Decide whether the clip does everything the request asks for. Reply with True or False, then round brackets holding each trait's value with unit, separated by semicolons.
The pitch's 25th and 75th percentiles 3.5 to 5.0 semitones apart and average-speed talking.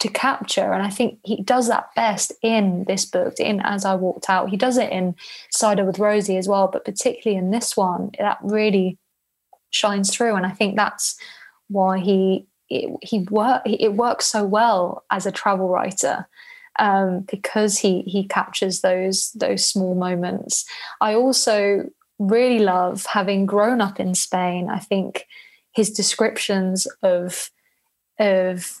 False (2.7 semitones; 160 wpm)